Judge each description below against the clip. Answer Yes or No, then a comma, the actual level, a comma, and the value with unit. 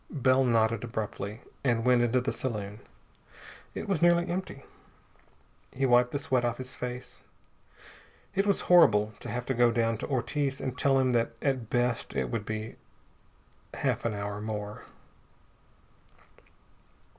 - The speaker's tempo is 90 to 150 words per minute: Yes, average, 145 wpm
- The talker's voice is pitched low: Yes, low, 120 Hz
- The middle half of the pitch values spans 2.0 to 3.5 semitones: Yes, average, 3.0 semitones